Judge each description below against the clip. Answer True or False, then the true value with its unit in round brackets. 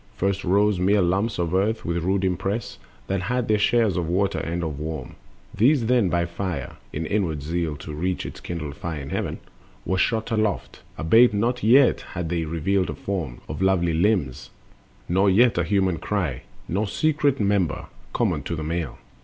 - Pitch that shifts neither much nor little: True (3.8 semitones)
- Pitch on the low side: True (95 Hz)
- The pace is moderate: True (180 wpm)